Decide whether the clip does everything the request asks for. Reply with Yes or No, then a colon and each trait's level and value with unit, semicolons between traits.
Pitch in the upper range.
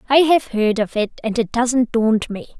Yes: high, 235 Hz